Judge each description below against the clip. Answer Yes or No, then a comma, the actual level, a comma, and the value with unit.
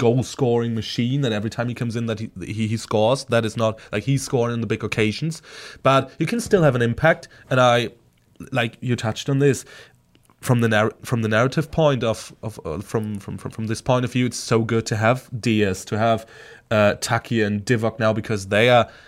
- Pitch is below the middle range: Yes, low, 115 Hz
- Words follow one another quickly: Yes, fast, 225 wpm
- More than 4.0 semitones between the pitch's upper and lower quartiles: No, narrow, 2.6 semitones